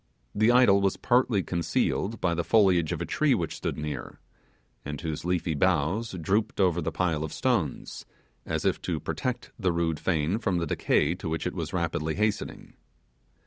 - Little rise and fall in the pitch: No, average, 4.2 semitones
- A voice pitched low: Yes, very low, 90 Hz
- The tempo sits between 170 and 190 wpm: Yes, average, 180 wpm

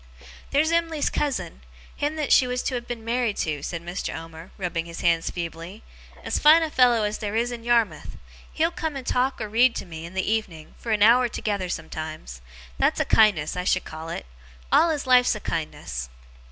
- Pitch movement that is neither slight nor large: No, wide, 7.0 semitones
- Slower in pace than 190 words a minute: No, fast, 205 wpm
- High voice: Yes, high, 215 Hz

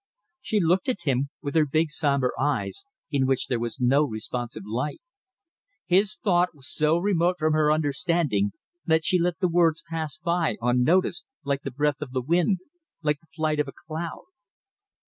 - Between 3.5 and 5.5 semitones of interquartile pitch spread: Yes, average, 3.9 semitones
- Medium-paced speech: Yes, average, 175 wpm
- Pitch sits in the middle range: Yes, medium, 155 Hz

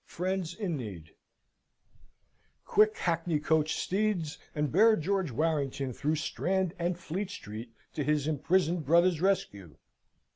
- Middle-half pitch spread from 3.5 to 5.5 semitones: Yes, average, 4.1 semitones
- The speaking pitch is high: No, medium, 165 Hz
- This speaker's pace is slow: Yes, slow, 115 wpm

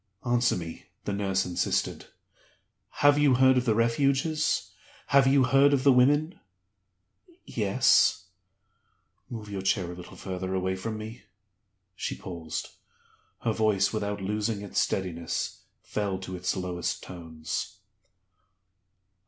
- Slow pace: Yes, slow, 125 wpm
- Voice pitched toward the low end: Yes, low, 105 Hz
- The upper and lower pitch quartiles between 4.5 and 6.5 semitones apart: Yes, average, 5.3 semitones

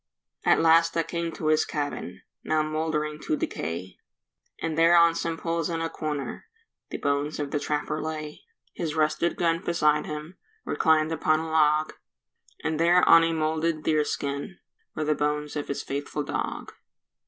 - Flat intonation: Yes, narrow, 1.7 semitones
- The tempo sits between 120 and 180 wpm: Yes, average, 165 wpm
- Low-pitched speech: No, medium, 155 Hz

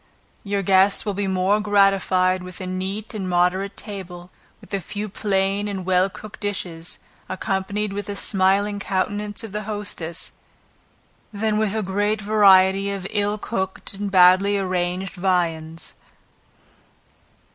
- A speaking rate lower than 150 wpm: Yes, slow, 135 wpm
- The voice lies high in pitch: Yes, high, 195 Hz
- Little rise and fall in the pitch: Yes, narrow, 1.8 semitones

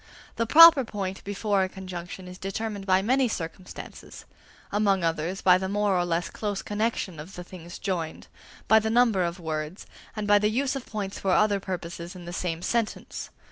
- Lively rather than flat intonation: No, average, 3.2 semitones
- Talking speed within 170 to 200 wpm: Yes, average, 185 wpm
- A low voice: No, high, 190 Hz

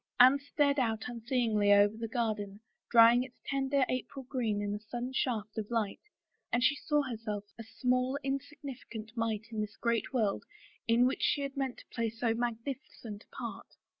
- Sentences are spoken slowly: No, average, 180 wpm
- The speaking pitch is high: Yes, high, 235 Hz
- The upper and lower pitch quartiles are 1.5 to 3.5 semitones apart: Yes, average, 3.2 semitones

